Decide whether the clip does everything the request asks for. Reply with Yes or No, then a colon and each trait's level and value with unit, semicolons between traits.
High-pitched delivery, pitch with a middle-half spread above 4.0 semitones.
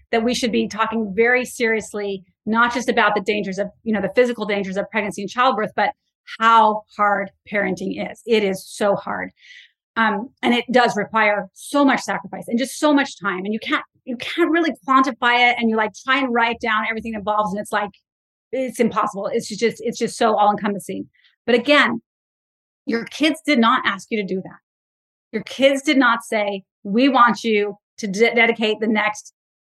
No: high, 225 Hz; average, 2.9 semitones